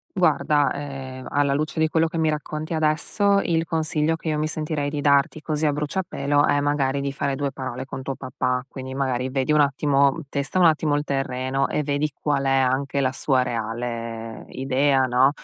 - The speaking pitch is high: No, medium, 140 Hz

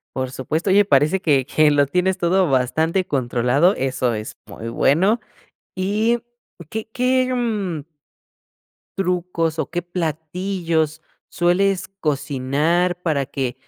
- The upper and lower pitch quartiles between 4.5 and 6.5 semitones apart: Yes, average, 4.9 semitones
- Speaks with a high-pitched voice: No, medium, 165 Hz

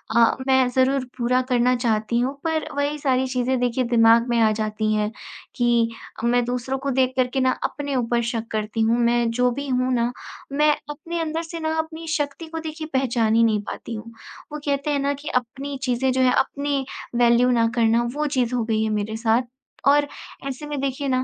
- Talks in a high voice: Yes, very high, 255 Hz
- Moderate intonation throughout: Yes, average, 3.1 semitones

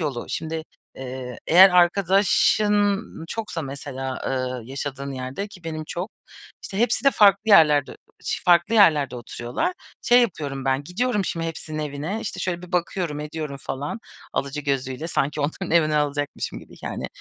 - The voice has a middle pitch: Yes, medium, 155 Hz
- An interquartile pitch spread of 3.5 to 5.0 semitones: No, wide, 5.4 semitones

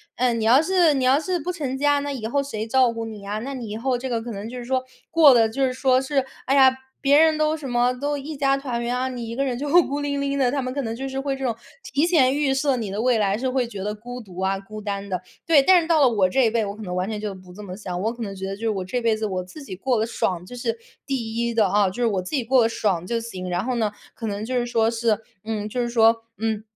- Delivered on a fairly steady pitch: No, average, 4.1 semitones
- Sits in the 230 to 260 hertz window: Yes, high, 240 Hz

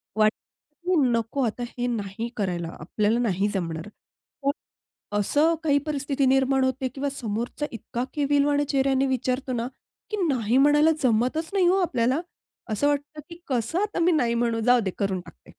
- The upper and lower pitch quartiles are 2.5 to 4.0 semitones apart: No, average, 4.4 semitones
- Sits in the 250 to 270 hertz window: Yes, very high, 255 Hz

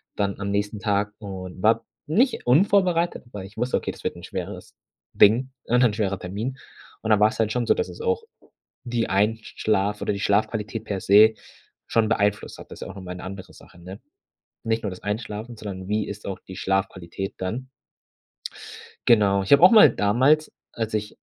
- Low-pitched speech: Yes, low, 105 Hz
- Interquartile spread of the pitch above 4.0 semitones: No, average, 2.9 semitones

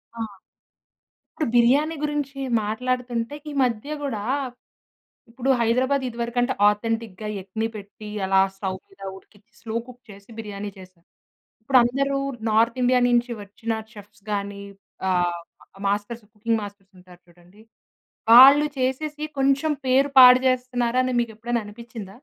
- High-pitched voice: Yes, high, 230 Hz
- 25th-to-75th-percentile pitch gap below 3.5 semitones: No, average, 3.8 semitones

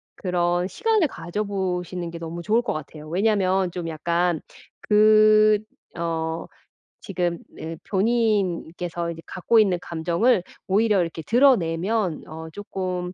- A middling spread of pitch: Yes, average, 3.9 semitones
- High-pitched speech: No, medium, 180 Hz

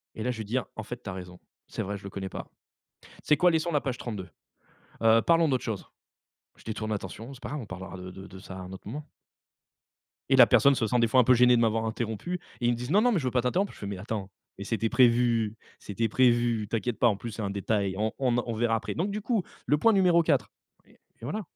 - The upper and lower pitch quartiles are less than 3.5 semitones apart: No, average, 4.0 semitones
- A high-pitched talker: No, low, 115 Hz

